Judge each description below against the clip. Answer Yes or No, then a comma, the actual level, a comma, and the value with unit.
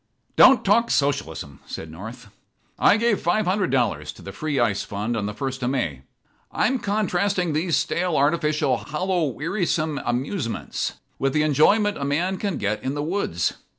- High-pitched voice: No, medium, 150 Hz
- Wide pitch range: Yes, wide, 7.4 semitones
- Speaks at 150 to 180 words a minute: Yes, average, 165 wpm